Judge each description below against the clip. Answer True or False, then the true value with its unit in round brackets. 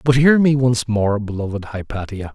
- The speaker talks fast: False (180 wpm)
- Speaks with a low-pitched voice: True (115 Hz)